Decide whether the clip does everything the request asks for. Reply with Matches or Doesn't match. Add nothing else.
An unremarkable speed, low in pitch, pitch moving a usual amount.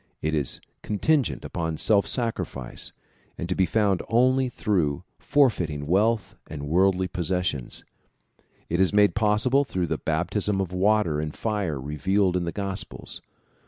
Matches